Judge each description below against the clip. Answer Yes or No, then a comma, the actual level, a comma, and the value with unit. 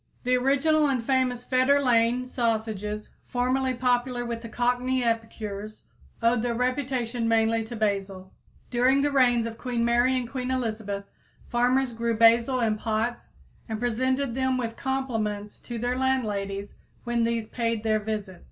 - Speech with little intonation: Yes, narrow, 2.3 semitones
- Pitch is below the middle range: No, high, 240 Hz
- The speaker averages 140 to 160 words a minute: Yes, average, 145 wpm